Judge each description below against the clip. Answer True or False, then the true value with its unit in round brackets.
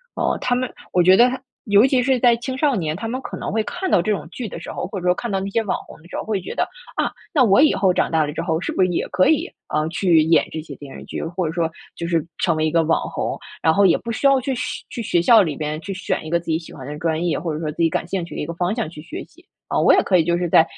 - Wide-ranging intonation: True (5.9 semitones)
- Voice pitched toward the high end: False (180 Hz)